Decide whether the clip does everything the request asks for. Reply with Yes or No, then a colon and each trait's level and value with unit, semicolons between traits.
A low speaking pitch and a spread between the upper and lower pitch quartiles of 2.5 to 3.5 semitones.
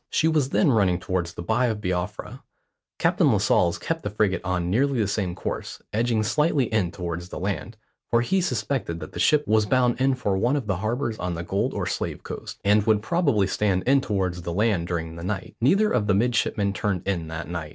No: low, 105 Hz; average, 5.3 semitones